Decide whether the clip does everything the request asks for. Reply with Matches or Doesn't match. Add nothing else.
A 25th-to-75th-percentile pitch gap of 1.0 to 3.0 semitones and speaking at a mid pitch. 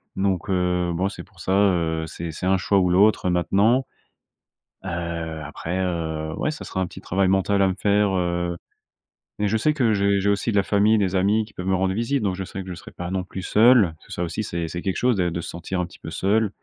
Doesn't match